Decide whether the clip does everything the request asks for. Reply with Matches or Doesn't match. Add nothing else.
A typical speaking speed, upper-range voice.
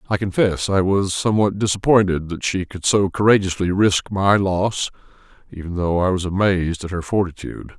Doesn't match